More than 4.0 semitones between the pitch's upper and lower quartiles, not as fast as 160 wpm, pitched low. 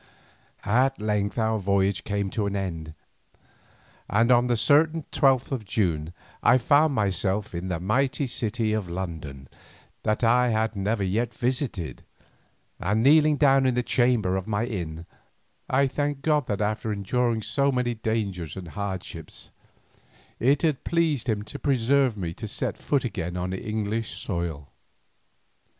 Yes: average, 4.9 semitones; average, 150 wpm; low, 110 Hz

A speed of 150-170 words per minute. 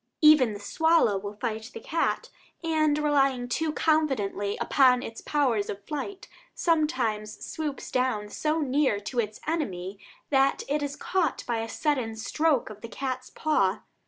Yes: average, 155 wpm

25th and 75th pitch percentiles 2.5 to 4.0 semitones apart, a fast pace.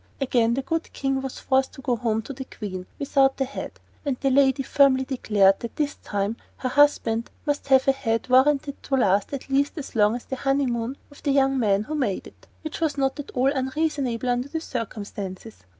Yes: average, 3.3 semitones; fast, 210 wpm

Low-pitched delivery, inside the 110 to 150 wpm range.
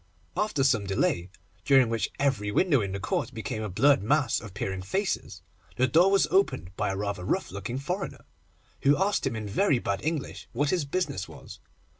No: low, 125 Hz; average, 190 wpm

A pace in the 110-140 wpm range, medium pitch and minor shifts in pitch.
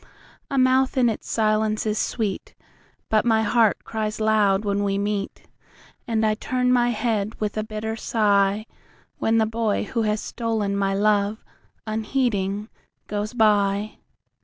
No: slow, 135 wpm; high, 215 Hz; narrow, 1.6 semitones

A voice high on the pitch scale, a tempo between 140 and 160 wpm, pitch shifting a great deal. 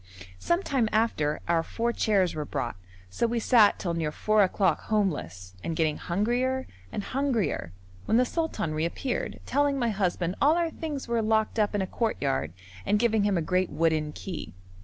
No: high, 210 Hz; average, 180 wpm; wide, 6.3 semitones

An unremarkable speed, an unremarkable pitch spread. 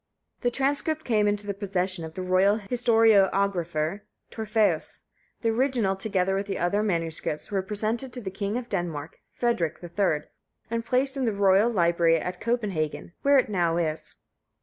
Yes: average, 155 wpm; average, 4.5 semitones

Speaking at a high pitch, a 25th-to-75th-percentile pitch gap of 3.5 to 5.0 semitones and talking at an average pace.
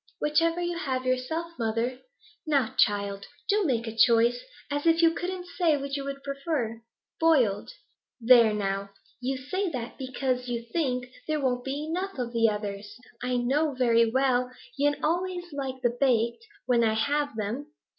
Yes: very high, 260 Hz; average, 4.5 semitones; average, 165 wpm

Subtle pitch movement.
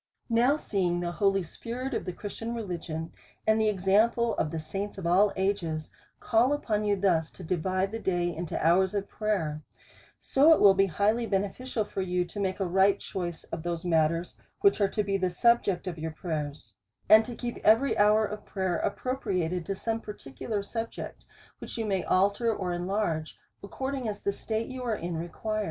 No: average, 3.9 semitones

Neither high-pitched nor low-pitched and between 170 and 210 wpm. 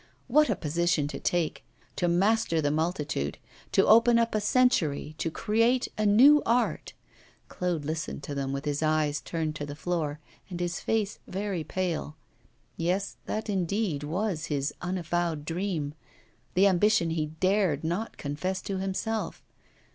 No: medium, 175 Hz; average, 150 wpm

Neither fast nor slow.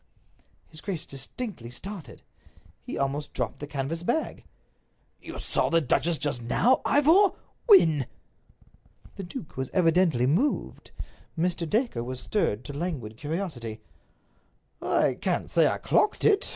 No: slow, 130 wpm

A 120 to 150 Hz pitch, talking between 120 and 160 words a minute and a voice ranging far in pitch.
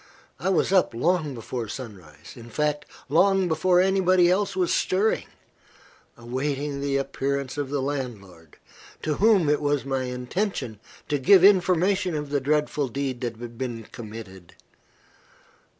Yes: medium, 140 Hz; average, 140 wpm; wide, 6.4 semitones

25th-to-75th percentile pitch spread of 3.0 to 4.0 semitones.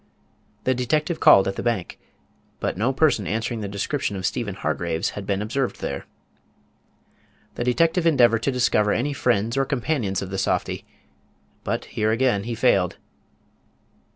No: average, 4.7 semitones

